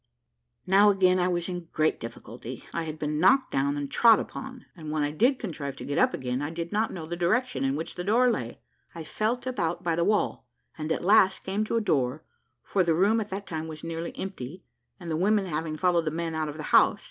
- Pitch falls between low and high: Yes, medium, 170 Hz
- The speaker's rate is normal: No, fast, 235 wpm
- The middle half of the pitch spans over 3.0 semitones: Yes, average, 4.3 semitones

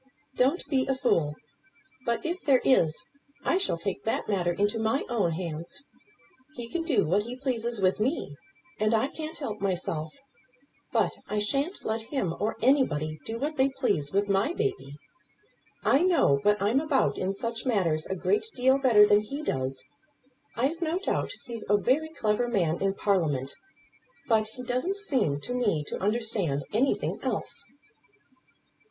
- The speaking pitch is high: Yes, high, 225 Hz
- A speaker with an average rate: Yes, average, 165 wpm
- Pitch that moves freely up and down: Yes, wide, 6.0 semitones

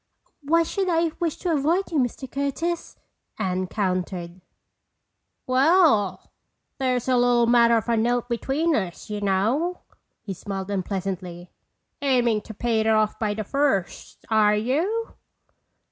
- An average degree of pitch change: No, wide, 5.8 semitones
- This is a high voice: Yes, high, 235 Hz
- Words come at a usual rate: No, slow, 130 wpm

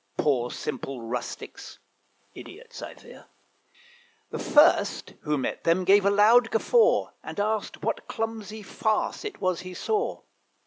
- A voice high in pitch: Yes, high, 205 Hz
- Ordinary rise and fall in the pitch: No, wide, 6.3 semitones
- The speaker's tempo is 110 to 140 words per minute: Yes, slow, 135 wpm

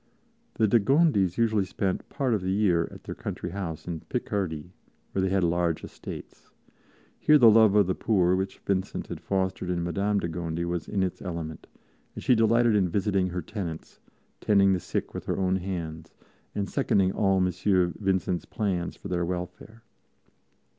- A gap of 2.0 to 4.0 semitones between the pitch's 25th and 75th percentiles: Yes, average, 2.8 semitones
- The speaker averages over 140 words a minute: Yes, average, 175 wpm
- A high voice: No, very low, 95 Hz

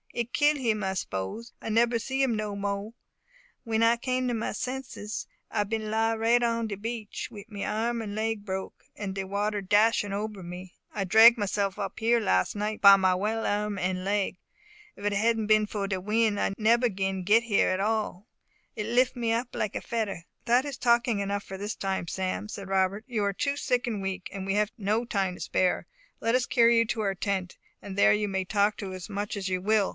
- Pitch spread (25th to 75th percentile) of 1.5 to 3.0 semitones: Yes, average, 2.7 semitones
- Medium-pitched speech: No, high, 210 Hz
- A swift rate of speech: Yes, fast, 220 wpm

